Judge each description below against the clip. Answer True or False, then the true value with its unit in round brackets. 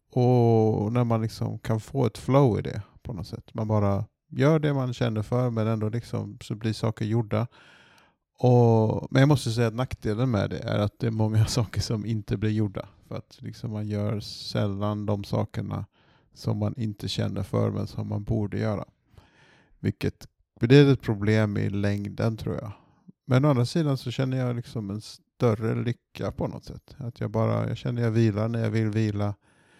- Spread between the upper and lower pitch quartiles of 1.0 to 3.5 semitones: True (2.5 semitones)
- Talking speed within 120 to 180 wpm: False (195 wpm)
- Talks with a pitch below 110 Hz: False (115 Hz)